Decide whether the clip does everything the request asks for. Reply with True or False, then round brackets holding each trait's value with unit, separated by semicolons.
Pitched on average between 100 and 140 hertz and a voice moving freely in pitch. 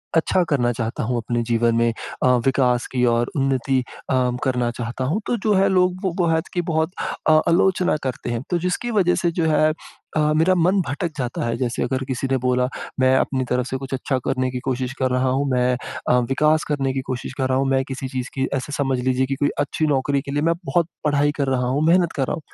False (135 Hz; 3.8 semitones)